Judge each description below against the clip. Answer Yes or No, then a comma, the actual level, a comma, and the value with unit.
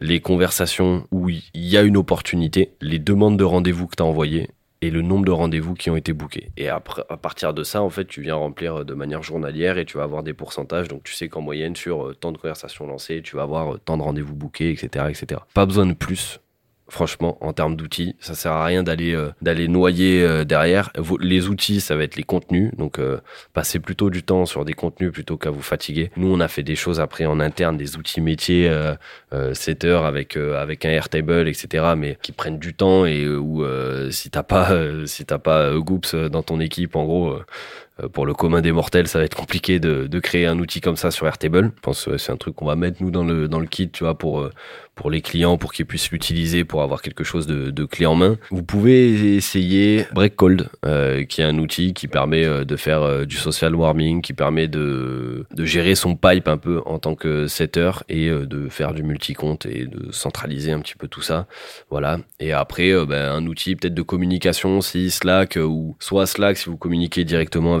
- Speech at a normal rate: No, fast, 235 wpm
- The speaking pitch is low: Yes, very low, 80 Hz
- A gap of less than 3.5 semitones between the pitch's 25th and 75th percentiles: Yes, average, 2.7 semitones